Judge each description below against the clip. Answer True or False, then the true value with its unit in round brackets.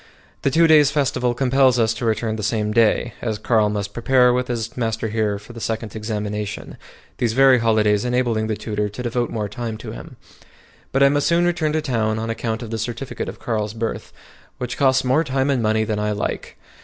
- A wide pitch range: False (2.8 semitones)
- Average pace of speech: False (210 wpm)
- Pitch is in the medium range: False (115 Hz)